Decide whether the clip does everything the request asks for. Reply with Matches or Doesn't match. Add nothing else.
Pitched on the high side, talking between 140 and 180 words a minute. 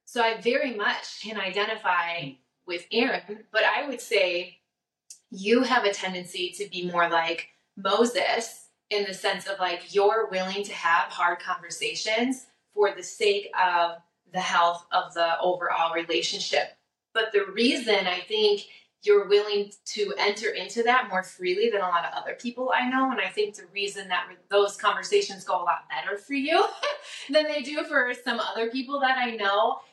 Matches